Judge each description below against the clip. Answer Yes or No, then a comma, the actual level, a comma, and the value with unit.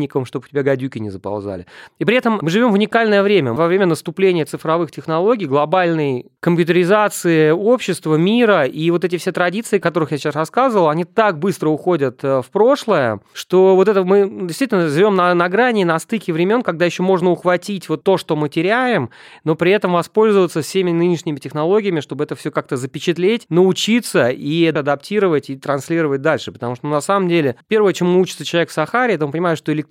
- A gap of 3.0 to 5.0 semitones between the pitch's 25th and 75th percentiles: Yes, average, 4.0 semitones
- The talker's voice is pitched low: No, medium, 170 Hz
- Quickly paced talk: Yes, fast, 190 wpm